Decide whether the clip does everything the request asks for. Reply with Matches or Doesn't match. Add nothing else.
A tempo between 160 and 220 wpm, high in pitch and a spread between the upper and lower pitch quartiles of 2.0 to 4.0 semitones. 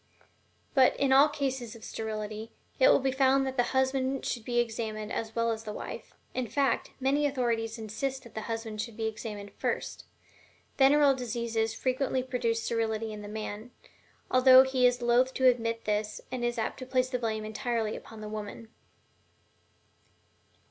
Matches